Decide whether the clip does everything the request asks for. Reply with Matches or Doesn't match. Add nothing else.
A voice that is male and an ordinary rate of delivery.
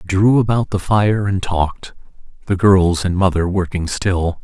Matches